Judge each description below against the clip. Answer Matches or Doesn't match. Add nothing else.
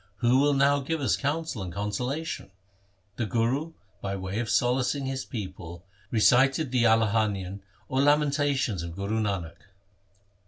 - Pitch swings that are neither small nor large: Doesn't match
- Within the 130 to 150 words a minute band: Matches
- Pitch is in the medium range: Doesn't match